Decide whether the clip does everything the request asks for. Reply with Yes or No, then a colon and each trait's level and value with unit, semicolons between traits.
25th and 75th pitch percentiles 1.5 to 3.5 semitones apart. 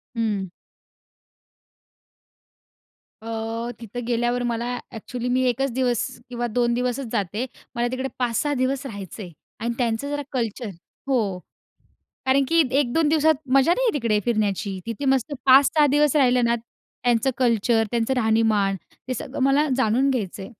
Yes: average, 3.1 semitones